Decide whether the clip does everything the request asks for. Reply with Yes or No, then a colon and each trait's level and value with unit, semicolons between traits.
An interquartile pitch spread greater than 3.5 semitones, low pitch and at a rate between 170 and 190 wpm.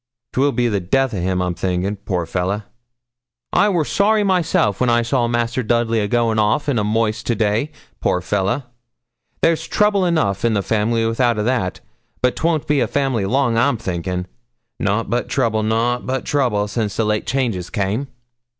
Yes: average, 4.2 semitones; low, 115 Hz; average, 185 wpm